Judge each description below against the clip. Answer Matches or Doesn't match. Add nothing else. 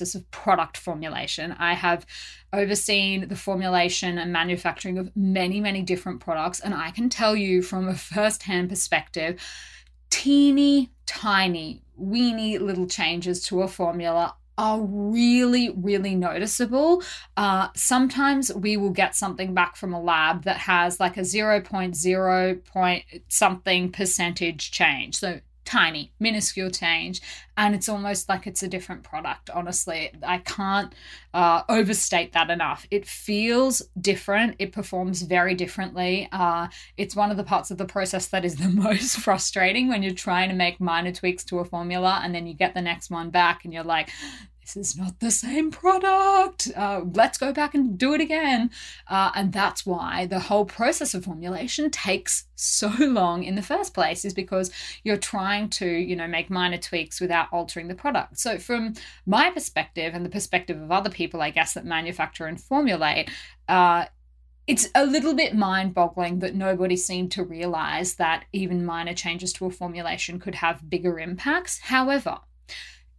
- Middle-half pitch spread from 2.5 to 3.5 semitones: Matches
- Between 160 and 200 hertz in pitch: Matches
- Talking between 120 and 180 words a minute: Matches